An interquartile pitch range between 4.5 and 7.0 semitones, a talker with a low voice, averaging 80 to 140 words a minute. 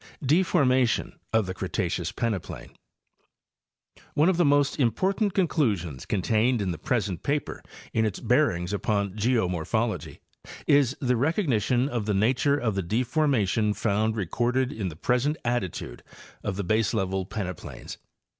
Yes: average, 5.2 semitones; low, 115 Hz; slow, 135 wpm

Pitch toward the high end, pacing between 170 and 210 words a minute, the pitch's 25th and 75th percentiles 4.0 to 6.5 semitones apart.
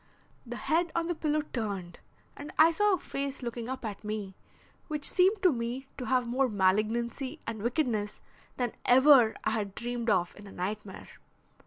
Yes: high, 240 Hz; average, 175 wpm; average, 5.3 semitones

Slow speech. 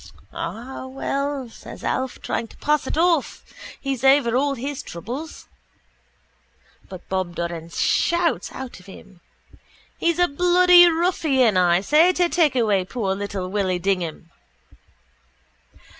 Yes: slow, 130 wpm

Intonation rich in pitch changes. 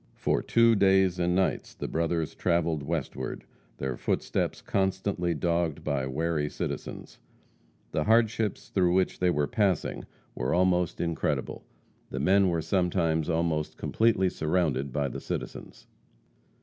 No: average, 3.5 semitones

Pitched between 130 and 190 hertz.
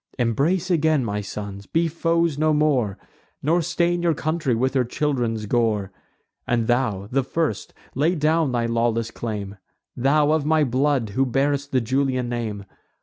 Yes: low, 135 Hz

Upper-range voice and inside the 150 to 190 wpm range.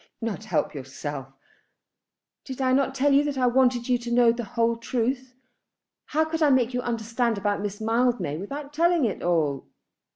Yes: high, 240 Hz; average, 175 wpm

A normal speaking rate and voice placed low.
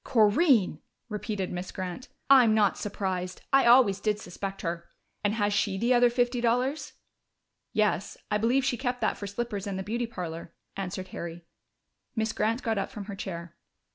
No: average, 170 wpm; high, 210 Hz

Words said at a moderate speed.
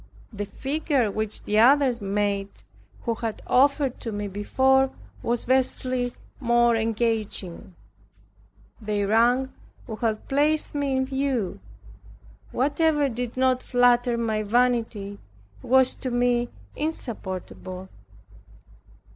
No: slow, 105 wpm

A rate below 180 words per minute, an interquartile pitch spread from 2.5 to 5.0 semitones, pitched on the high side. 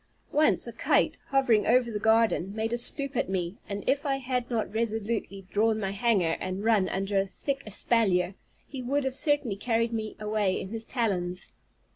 No: average, 185 wpm; average, 3.8 semitones; high, 220 Hz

